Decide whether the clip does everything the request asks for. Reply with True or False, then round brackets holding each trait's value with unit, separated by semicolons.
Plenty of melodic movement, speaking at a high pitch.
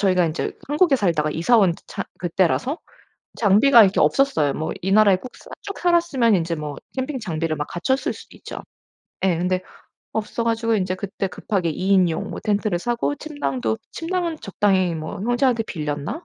True (6.4 semitones; 200 Hz)